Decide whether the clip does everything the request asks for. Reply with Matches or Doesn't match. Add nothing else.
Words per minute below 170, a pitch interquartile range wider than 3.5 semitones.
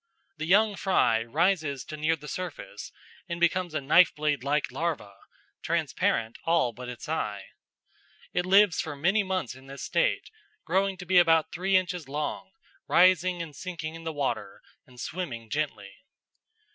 Matches